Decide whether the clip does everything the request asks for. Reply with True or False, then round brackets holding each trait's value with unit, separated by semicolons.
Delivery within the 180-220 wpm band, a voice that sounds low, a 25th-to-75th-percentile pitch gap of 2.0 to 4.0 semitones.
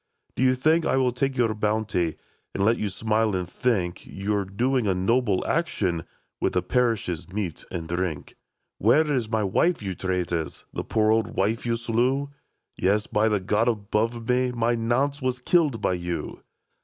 False (185 wpm; 110 Hz; 4.5 semitones)